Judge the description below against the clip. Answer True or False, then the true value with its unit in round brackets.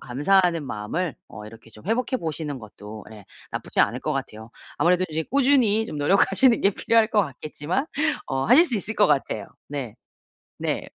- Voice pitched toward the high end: False (160 Hz)